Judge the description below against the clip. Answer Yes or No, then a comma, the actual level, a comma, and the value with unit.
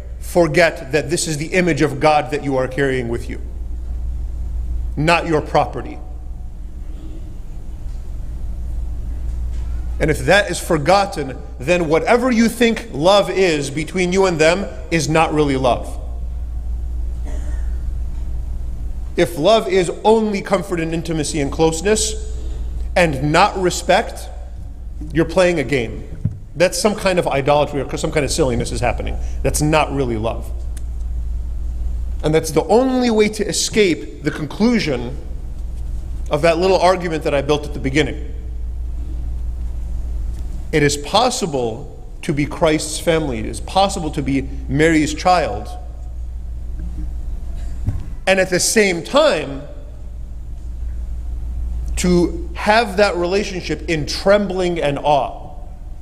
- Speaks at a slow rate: Yes, slow, 120 wpm